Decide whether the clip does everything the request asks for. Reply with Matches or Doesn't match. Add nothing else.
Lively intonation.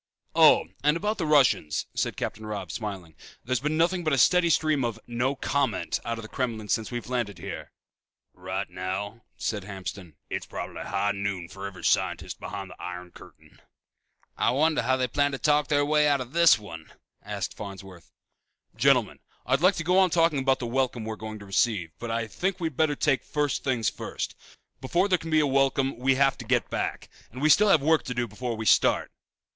Matches